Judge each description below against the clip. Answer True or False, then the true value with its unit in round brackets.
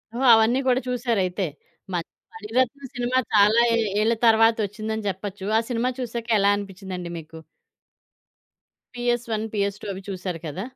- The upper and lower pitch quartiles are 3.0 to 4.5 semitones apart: True (3.7 semitones)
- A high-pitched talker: True (220 Hz)